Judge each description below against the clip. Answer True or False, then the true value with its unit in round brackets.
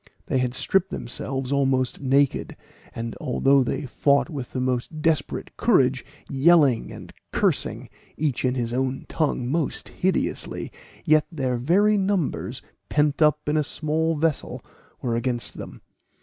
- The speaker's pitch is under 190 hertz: True (140 Hz)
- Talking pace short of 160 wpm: True (140 wpm)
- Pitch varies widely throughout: False (3.4 semitones)